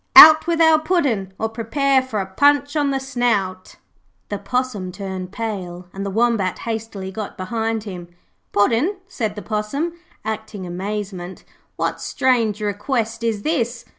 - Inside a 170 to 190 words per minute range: No, average, 145 wpm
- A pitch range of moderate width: Yes, average, 4.8 semitones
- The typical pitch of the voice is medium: No, high, 220 Hz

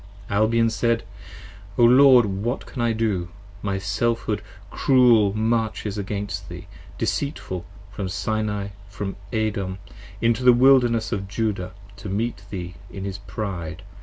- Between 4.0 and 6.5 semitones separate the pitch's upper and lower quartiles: No, average, 2.9 semitones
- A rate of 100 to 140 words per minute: Yes, slow, 135 wpm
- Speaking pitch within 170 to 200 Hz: No, low, 105 Hz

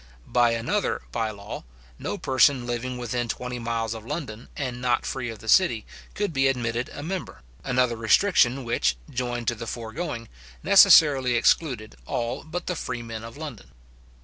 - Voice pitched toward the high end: No, low, 120 Hz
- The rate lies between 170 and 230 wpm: No, average, 160 wpm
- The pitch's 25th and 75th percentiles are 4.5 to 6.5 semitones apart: No, narrow, 2.5 semitones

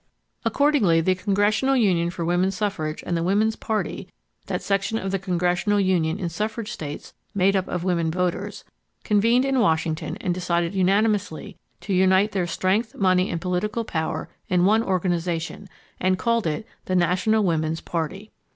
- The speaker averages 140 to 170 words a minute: Yes, average, 160 wpm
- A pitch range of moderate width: Yes, average, 3.3 semitones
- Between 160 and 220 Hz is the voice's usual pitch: Yes, medium, 185 Hz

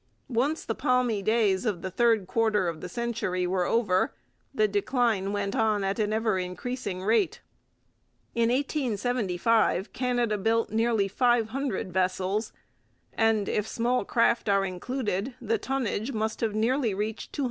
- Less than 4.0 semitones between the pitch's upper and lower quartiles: Yes, average, 3.4 semitones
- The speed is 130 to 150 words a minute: Yes, average, 145 wpm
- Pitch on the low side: No, high, 220 Hz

